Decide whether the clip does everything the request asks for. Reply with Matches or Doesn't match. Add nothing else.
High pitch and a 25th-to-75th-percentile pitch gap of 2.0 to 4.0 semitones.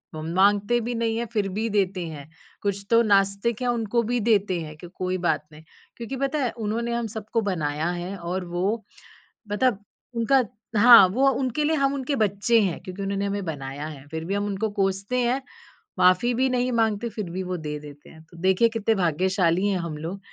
Doesn't match